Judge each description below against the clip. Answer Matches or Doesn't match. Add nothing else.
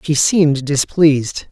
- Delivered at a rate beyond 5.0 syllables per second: Doesn't match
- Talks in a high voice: Doesn't match